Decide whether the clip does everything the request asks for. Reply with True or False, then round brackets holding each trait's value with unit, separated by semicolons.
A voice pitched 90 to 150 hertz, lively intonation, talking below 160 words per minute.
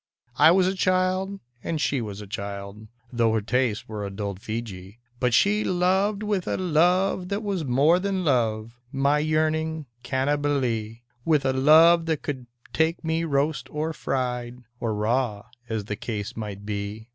False (135 Hz; 6.9 semitones; 170 wpm)